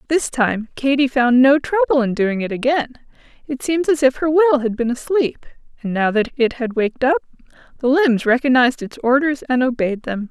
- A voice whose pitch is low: No, very high, 260 Hz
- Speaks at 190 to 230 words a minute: Yes, average, 200 wpm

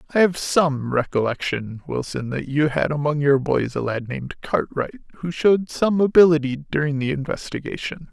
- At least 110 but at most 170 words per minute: Yes, average, 165 wpm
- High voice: No, medium, 145 Hz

